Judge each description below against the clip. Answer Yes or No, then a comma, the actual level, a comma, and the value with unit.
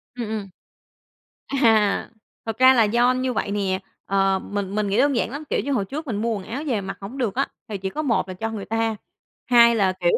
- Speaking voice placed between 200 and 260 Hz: Yes, high, 220 Hz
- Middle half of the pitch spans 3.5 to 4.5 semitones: Yes, average, 4.1 semitones